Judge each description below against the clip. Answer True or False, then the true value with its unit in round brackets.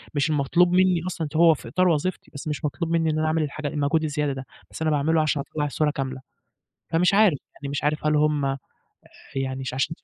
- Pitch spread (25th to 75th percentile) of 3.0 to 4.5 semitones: False (2.4 semitones)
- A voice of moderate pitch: True (150 Hz)